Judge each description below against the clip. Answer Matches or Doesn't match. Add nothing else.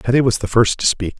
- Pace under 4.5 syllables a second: Doesn't match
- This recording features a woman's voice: Doesn't match